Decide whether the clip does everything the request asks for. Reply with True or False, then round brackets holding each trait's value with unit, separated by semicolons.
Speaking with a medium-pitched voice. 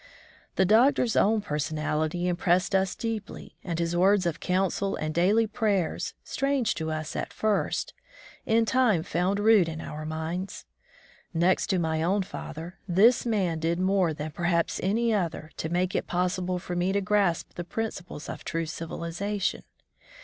True (180 Hz)